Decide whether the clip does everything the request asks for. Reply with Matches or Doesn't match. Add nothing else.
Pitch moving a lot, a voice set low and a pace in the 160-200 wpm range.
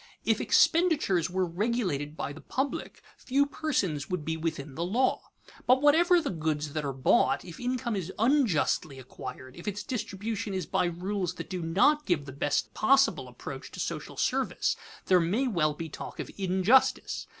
Doesn't match